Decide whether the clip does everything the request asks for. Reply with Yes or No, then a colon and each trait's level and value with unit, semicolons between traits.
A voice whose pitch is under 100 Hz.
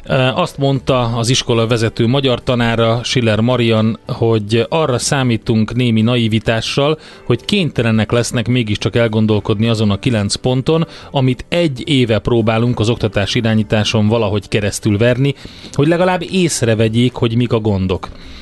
No: low, 115 Hz